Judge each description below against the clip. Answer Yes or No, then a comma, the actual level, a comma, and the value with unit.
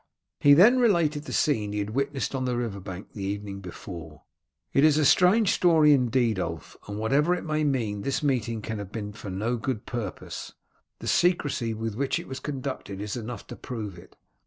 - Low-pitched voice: Yes, low, 120 Hz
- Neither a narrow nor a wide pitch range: No, wide, 6.0 semitones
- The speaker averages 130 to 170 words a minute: No, average, 200 wpm